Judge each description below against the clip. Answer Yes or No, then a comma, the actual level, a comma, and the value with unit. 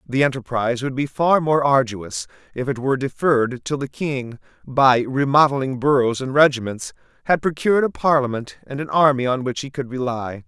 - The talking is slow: No, average, 180 wpm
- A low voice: Yes, low, 130 Hz